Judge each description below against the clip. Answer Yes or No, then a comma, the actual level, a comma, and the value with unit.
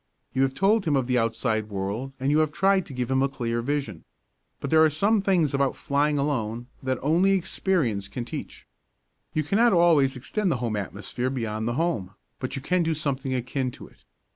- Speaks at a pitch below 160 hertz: Yes, low, 135 Hz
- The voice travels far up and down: No, average, 4.9 semitones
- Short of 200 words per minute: No, fast, 205 wpm